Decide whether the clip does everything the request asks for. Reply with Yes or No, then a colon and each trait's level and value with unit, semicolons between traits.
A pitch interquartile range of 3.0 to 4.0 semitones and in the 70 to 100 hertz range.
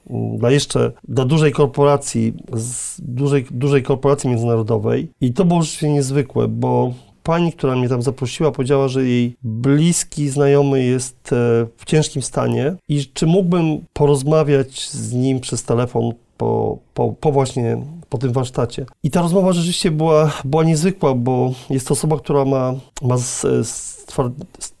No: average, 3.4 semitones; medium, 140 Hz